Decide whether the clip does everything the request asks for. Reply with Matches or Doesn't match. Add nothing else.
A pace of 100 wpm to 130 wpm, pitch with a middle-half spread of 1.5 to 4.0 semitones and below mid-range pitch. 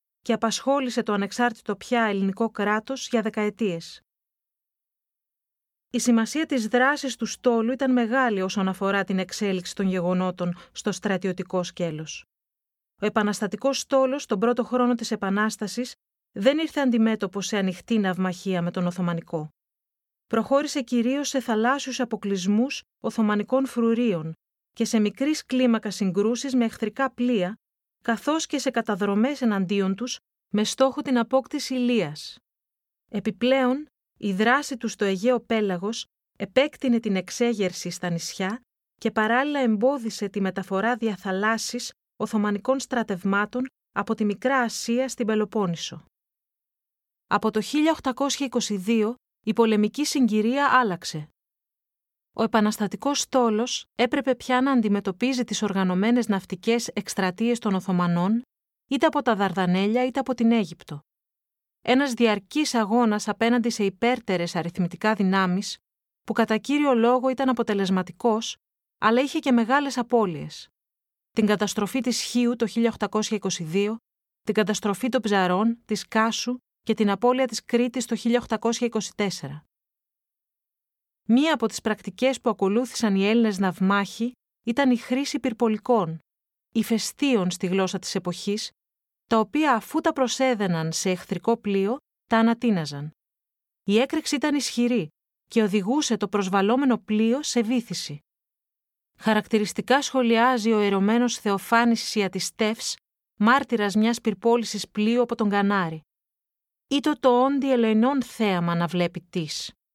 Doesn't match